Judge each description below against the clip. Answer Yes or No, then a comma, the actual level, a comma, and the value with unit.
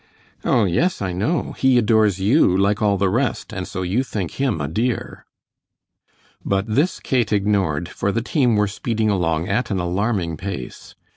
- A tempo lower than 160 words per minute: No, average, 170 wpm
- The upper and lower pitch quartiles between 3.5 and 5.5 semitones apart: Yes, average, 4.1 semitones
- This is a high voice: No, low, 105 Hz